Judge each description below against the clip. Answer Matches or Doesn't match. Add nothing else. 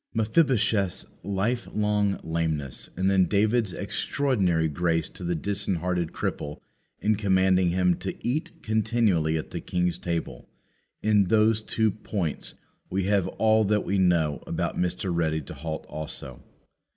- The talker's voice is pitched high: Doesn't match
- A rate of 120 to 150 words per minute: Matches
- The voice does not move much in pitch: Doesn't match